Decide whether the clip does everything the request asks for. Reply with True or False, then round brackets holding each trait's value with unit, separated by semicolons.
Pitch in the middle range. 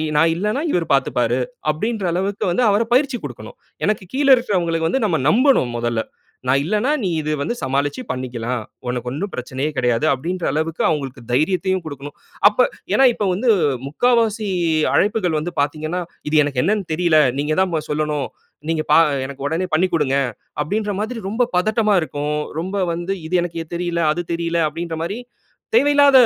True (170 Hz)